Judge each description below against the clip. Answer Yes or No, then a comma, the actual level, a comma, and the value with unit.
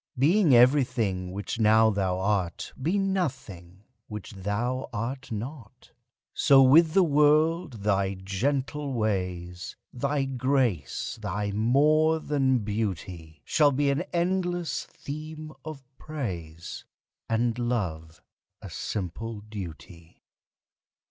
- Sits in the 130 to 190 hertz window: No, low, 120 Hz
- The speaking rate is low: Yes, slow, 105 wpm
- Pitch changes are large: Yes, wide, 7.0 semitones